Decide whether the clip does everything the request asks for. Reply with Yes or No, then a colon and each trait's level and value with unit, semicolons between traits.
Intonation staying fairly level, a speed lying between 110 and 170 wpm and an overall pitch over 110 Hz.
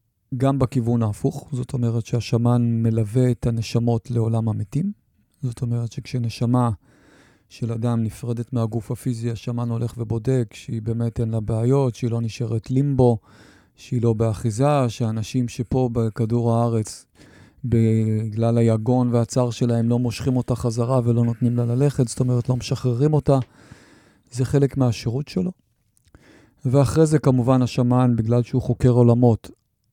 Yes: narrow, 1.8 semitones; slow, 135 wpm; low, 120 Hz